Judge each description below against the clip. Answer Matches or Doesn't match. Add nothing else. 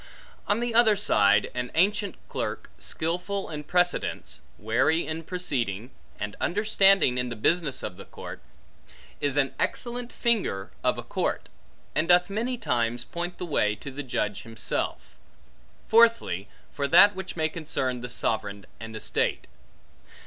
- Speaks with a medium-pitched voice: Matches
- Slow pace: Doesn't match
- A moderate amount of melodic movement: Doesn't match